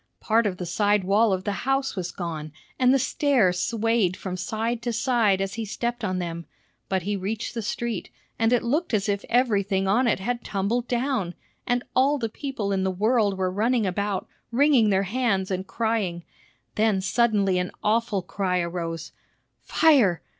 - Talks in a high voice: Yes, high, 210 Hz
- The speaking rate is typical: Yes, average, 180 wpm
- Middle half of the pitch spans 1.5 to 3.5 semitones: No, average, 3.9 semitones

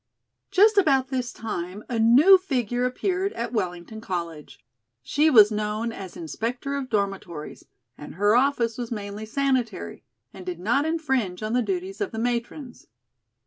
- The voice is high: Yes, high, 235 Hz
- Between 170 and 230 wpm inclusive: No, average, 150 wpm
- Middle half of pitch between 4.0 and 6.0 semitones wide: Yes, average, 5.3 semitones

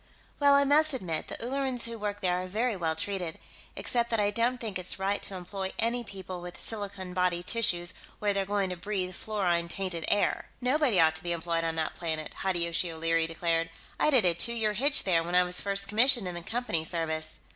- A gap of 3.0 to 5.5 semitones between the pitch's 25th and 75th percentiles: Yes, average, 4.6 semitones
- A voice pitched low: No, high, 190 Hz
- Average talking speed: No, fast, 215 wpm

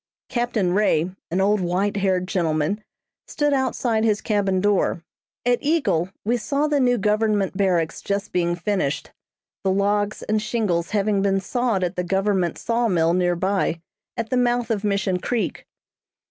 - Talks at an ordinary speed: Yes, average, 160 wpm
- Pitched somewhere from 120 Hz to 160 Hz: No, high, 200 Hz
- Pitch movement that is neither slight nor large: Yes, average, 3.5 semitones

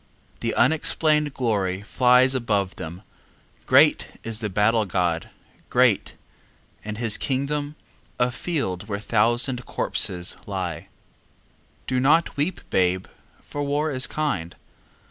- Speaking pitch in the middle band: No, low, 115 Hz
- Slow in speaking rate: Yes, slow, 120 wpm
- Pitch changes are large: Yes, wide, 6.4 semitones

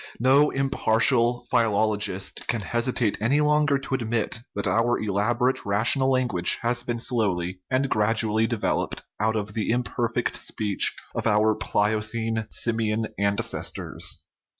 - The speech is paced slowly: Yes, slow, 125 wpm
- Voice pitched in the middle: No, low, 115 Hz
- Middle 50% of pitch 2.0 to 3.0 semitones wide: Yes, narrow, 2.5 semitones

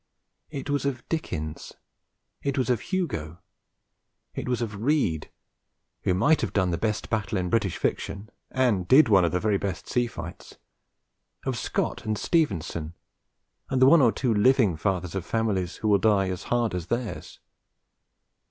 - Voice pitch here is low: Yes, low, 105 Hz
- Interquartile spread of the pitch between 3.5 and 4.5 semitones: No, wide, 5.6 semitones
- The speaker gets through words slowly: No, average, 165 wpm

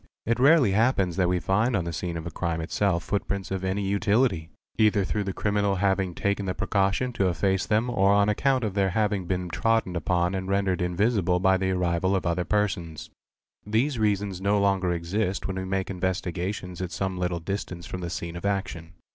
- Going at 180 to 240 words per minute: Yes, average, 200 wpm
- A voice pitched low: Yes, very low, 95 Hz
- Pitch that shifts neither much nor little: No, narrow, 2.3 semitones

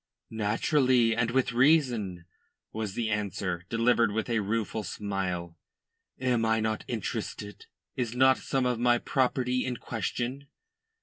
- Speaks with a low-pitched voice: Yes, low, 115 Hz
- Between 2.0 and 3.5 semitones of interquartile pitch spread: Yes, average, 3.1 semitones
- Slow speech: Yes, slow, 130 wpm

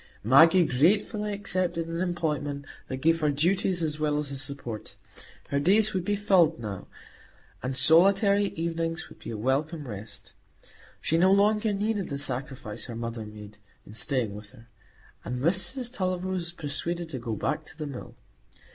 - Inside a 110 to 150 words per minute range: No, average, 165 wpm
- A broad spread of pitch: Yes, wide, 6.0 semitones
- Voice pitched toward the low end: No, medium, 160 Hz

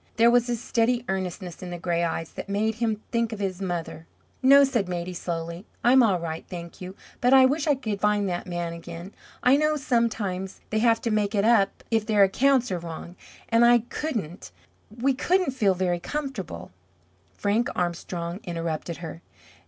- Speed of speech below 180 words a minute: No, average, 185 wpm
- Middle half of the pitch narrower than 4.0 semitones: No, wide, 5.4 semitones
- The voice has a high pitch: Yes, high, 200 Hz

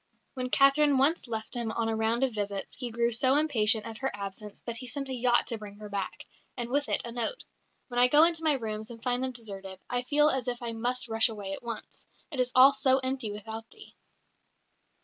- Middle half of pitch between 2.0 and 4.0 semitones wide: Yes, average, 3.1 semitones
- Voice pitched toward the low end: No, high, 240 Hz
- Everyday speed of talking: No, fast, 230 wpm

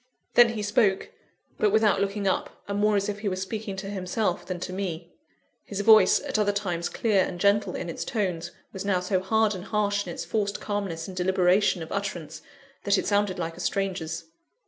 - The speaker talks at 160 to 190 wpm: No, fast, 205 wpm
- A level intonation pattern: Yes, narrow, 2.2 semitones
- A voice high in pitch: Yes, high, 195 Hz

